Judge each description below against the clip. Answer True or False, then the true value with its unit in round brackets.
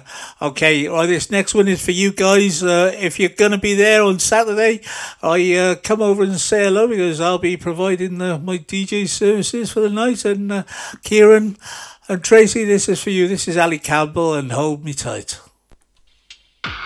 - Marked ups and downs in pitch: False (3.3 semitones)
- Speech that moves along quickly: False (185 wpm)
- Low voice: False (190 Hz)